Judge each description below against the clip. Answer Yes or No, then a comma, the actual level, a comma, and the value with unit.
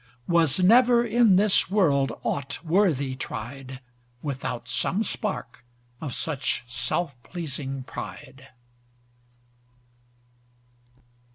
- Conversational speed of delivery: No, slow, 85 wpm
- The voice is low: No, medium, 150 Hz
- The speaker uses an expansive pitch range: Yes, wide, 6.1 semitones